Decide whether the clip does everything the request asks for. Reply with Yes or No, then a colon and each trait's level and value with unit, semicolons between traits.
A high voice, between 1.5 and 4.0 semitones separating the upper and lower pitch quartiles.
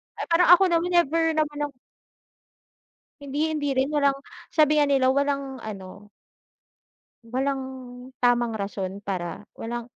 No: very high, 275 Hz; average, 4.7 semitones